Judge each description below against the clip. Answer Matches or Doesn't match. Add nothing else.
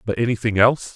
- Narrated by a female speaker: Doesn't match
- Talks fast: Doesn't match